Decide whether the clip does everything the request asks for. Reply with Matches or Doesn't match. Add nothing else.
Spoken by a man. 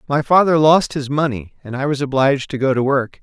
Matches